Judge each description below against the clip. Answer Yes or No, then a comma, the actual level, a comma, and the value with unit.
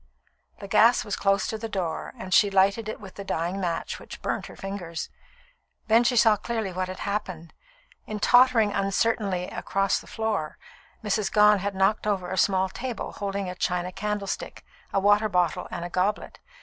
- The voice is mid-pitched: No, high, 200 Hz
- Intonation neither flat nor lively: No, narrow, 2.3 semitones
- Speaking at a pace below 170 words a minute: No, average, 180 wpm